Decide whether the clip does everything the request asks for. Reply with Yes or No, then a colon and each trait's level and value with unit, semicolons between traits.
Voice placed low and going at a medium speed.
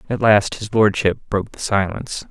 Yes: low, 105 Hz; average, 180 wpm